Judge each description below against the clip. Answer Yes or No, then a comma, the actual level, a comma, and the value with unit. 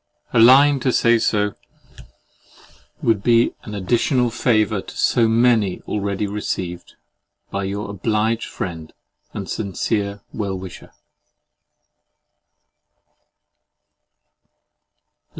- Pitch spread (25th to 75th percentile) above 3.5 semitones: No, average, 2.8 semitones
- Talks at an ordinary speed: No, slow, 90 wpm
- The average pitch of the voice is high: No, low, 105 Hz